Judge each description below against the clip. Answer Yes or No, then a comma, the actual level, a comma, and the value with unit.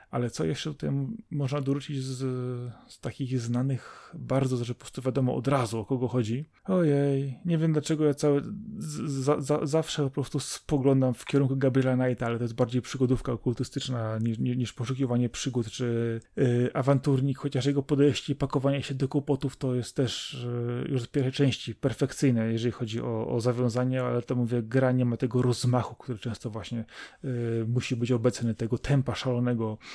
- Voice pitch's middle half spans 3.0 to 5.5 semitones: No, narrow, 2.5 semitones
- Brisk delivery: Yes, fast, 180 wpm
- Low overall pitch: Yes, low, 130 Hz